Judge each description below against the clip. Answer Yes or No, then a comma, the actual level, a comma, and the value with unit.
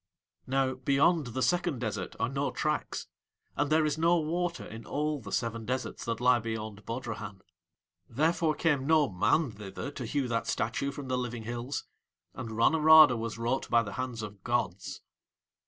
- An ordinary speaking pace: Yes, average, 170 wpm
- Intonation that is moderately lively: Yes, average, 4.6 semitones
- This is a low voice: Yes, low, 125 Hz